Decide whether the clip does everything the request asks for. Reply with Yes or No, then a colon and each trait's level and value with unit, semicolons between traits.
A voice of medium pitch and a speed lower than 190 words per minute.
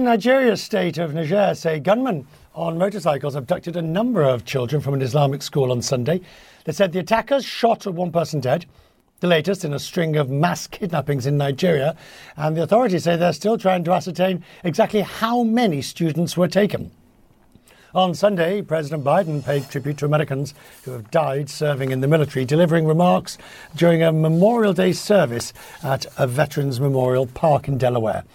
Yes: medium, 165 Hz; average, 175 wpm